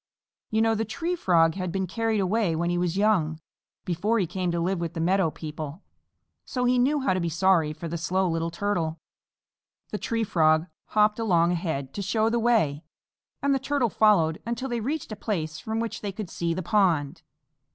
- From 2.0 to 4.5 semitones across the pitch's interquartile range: No, average, 5.0 semitones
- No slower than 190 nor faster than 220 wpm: Yes, fast, 205 wpm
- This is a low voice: No, medium, 185 Hz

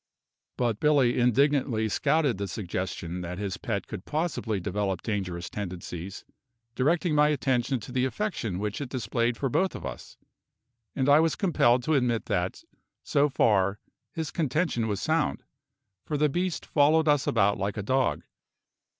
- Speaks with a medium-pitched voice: No, low, 120 Hz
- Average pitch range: No, wide, 6.5 semitones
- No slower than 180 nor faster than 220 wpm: No, average, 155 wpm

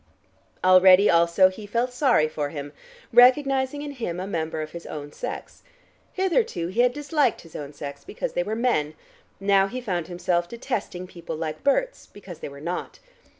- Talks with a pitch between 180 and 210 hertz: Yes, medium, 185 Hz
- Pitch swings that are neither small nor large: No, wide, 7.0 semitones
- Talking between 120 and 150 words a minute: No, average, 175 wpm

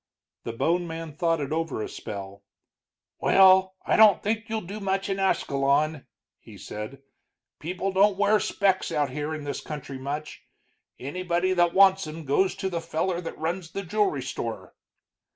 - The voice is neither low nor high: Yes, medium, 170 Hz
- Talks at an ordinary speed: Yes, average, 165 wpm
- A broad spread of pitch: No, average, 4.6 semitones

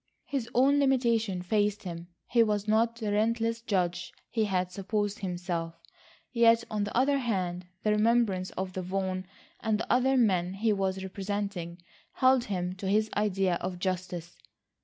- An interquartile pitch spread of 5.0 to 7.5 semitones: No, average, 3.7 semitones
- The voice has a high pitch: Yes, high, 205 Hz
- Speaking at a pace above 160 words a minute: No, average, 155 wpm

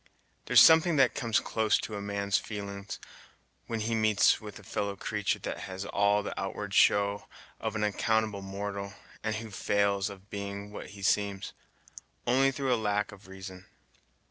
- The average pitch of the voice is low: Yes, low, 100 Hz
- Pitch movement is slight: Yes, narrow, 1.6 semitones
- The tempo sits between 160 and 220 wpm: Yes, average, 170 wpm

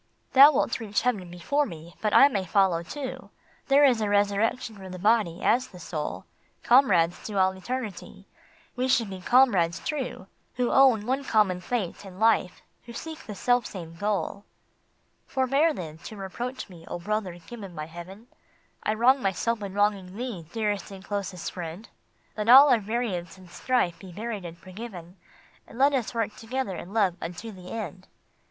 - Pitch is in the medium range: No, high, 205 Hz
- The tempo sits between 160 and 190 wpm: Yes, average, 175 wpm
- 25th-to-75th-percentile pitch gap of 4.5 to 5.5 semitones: Yes, average, 4.9 semitones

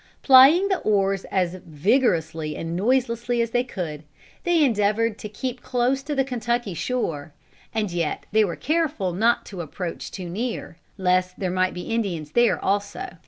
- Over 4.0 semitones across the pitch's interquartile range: Yes, wide, 5.5 semitones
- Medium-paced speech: Yes, average, 165 wpm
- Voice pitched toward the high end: Yes, high, 210 Hz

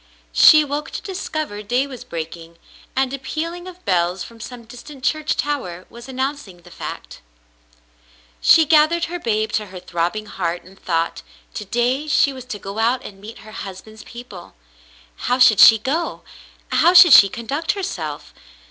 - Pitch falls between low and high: No, high, 235 Hz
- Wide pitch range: Yes, wide, 7.1 semitones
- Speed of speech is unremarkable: Yes, average, 165 wpm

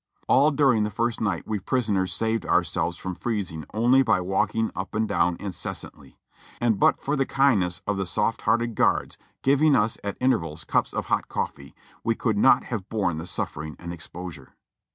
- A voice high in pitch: No, low, 105 Hz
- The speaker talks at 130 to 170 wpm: No, average, 180 wpm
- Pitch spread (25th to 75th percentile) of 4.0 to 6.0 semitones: Yes, average, 4.8 semitones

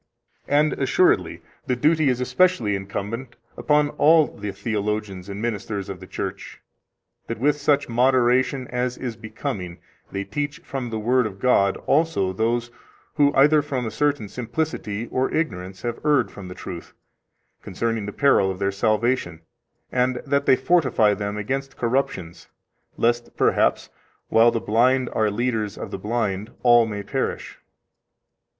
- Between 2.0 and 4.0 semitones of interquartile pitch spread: No, average, 4.6 semitones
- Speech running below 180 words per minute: Yes, average, 150 wpm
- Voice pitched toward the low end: Yes, low, 120 Hz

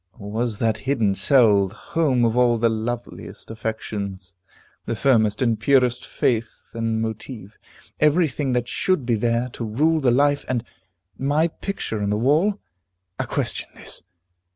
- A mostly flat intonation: No, average, 3.7 semitones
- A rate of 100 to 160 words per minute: Yes, average, 155 wpm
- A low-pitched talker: Yes, low, 120 Hz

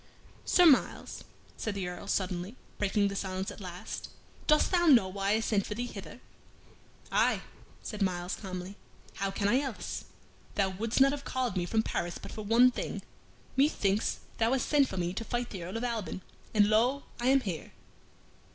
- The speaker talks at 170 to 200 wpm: Yes, average, 185 wpm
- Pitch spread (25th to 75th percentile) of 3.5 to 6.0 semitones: Yes, average, 4.5 semitones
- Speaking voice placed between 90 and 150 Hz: No, high, 210 Hz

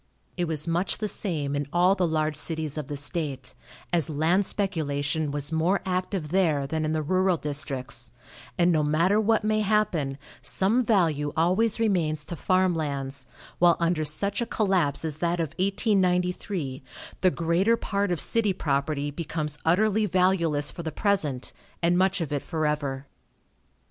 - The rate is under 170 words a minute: Yes, average, 160 wpm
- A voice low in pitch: No, medium, 165 Hz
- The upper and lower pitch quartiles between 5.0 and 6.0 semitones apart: No, average, 4.2 semitones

